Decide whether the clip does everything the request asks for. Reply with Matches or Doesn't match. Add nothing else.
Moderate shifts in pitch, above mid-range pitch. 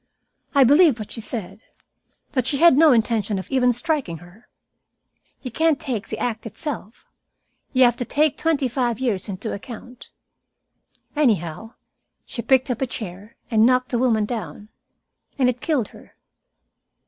Matches